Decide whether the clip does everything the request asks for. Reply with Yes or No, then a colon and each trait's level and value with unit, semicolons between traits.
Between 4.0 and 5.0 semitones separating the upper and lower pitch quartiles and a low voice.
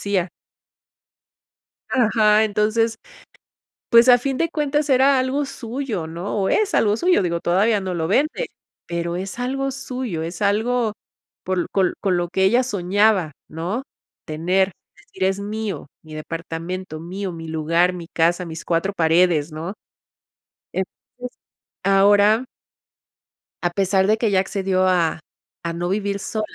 No: average, 4.6 semitones; high, 195 Hz